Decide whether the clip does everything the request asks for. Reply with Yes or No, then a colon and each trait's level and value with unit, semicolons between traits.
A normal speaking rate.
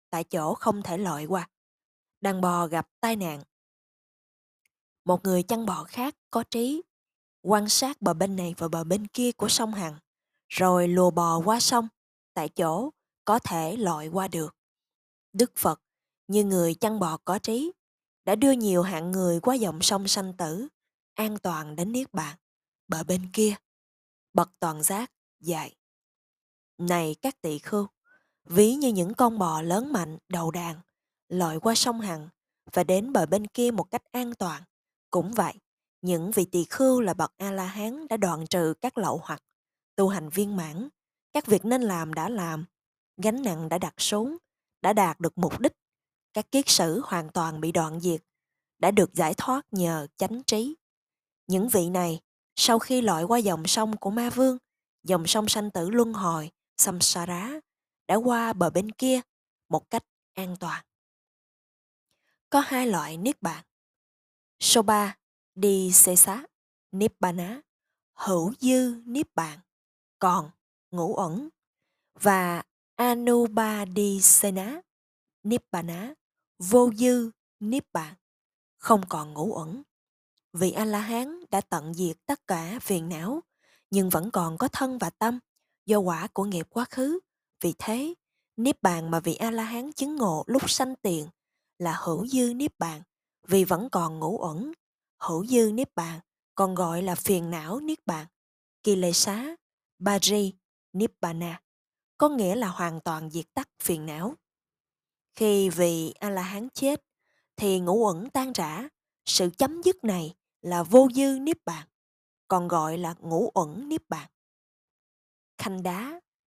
No: slow, 160 wpm